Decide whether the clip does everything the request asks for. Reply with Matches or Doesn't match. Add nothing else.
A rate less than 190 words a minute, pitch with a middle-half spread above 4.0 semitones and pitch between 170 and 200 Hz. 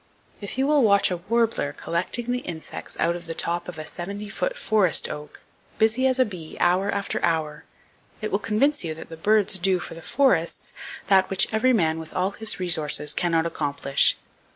Doesn't match